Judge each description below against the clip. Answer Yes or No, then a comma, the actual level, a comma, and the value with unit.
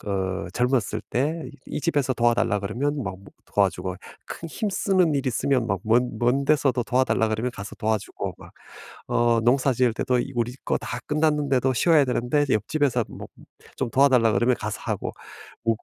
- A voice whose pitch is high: No, low, 125 Hz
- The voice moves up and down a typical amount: Yes, average, 3.6 semitones